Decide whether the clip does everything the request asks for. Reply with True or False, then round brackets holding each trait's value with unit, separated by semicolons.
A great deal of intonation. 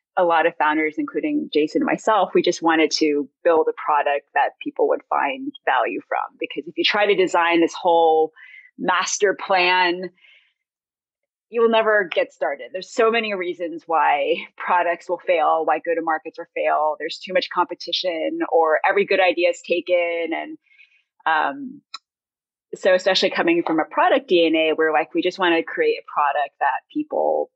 True (7.9 semitones)